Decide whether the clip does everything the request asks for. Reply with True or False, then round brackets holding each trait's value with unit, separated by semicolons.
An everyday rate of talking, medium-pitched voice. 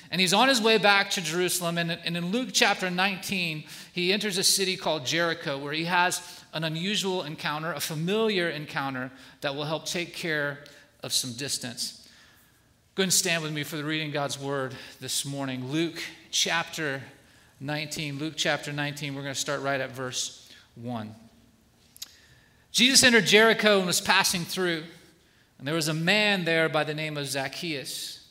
True (175 wpm; 160 Hz)